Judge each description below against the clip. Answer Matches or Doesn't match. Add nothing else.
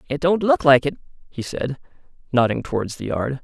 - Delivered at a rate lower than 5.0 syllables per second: Doesn't match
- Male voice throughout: Matches